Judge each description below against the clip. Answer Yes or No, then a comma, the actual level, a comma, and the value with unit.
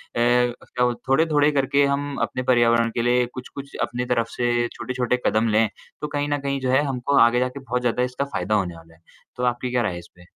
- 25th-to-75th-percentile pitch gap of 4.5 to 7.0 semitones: No, narrow, 2.4 semitones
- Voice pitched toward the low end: Yes, low, 125 Hz